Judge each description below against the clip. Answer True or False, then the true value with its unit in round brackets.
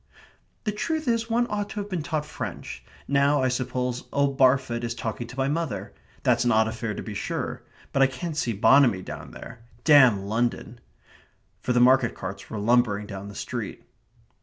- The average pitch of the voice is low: True (125 Hz)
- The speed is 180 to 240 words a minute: True (185 wpm)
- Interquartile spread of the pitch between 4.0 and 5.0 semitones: True (4.5 semitones)